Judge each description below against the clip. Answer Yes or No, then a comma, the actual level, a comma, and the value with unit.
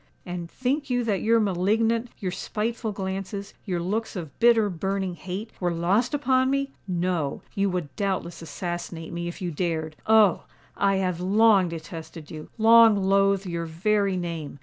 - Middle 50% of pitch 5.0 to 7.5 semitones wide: No, average, 4.1 semitones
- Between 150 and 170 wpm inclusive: No, average, 140 wpm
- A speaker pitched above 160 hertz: Yes, high, 190 Hz